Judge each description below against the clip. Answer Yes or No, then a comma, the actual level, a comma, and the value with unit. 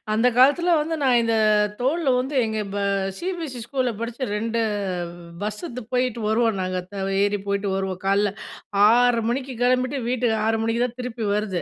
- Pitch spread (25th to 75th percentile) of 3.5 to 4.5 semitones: No, average, 3.0 semitones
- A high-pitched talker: Yes, high, 240 Hz